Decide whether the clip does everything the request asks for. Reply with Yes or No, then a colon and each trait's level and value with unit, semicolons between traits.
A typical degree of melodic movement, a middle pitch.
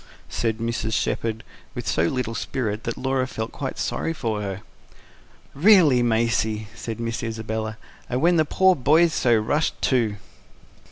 No: average, 3.4 semitones; low, 115 Hz